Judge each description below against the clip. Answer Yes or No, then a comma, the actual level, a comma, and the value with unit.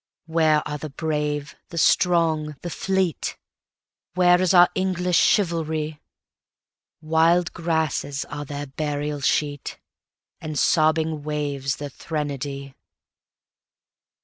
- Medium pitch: Yes, medium, 155 Hz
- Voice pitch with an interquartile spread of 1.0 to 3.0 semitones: Yes, narrow, 2.4 semitones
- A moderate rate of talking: No, slow, 90 wpm